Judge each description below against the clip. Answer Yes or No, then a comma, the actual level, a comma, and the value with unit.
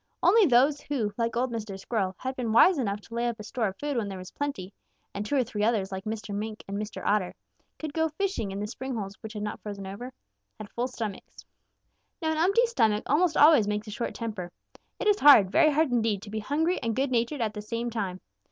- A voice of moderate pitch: No, high, 230 Hz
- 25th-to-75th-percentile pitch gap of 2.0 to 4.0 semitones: No, average, 5.2 semitones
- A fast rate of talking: Yes, fast, 245 wpm